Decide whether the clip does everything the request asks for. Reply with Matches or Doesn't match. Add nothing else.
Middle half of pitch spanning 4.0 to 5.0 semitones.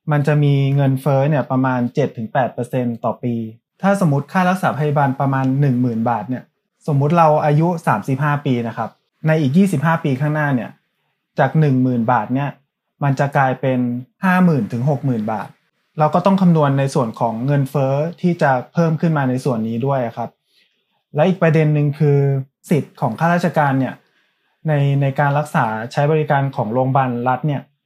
Doesn't match